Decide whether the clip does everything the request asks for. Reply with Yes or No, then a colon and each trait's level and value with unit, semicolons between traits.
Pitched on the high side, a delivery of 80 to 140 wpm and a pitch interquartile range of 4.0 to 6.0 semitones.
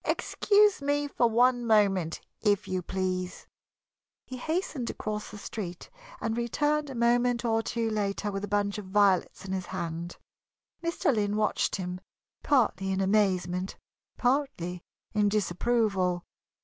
Yes: high, 210 Hz; slow, 135 wpm; average, 4.4 semitones